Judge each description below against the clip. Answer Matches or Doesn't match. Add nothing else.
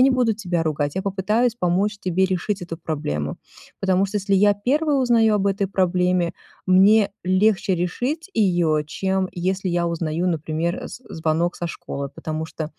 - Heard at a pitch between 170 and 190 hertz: Matches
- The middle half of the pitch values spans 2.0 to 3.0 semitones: Doesn't match